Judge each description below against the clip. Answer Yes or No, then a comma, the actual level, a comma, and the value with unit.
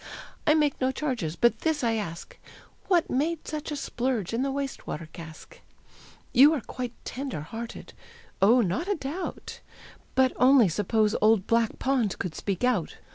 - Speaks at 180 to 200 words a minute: No, average, 165 wpm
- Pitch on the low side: No, very high, 250 Hz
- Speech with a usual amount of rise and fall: Yes, average, 5.0 semitones